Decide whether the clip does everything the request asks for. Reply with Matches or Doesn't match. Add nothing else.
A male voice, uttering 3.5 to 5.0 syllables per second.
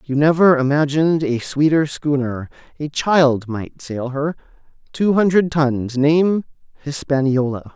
Matches